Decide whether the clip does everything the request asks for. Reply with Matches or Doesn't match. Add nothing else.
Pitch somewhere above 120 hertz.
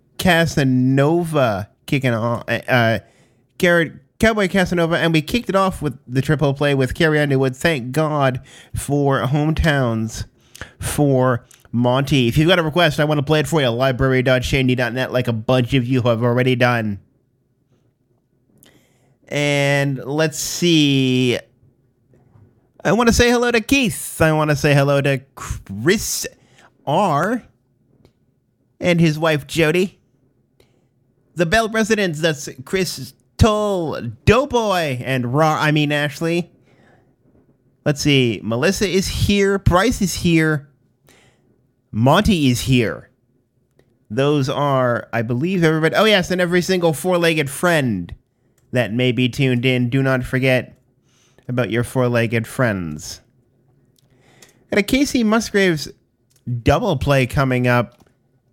Matches